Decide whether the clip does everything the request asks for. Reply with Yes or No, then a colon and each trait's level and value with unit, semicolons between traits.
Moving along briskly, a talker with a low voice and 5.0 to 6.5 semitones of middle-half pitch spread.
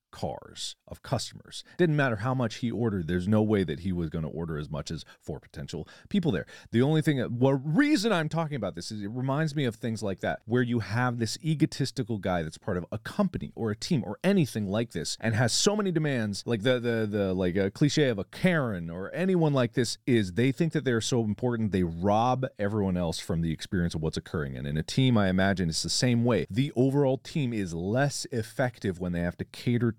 Yes: fast, 235 wpm; low, 115 Hz; wide, 5.5 semitones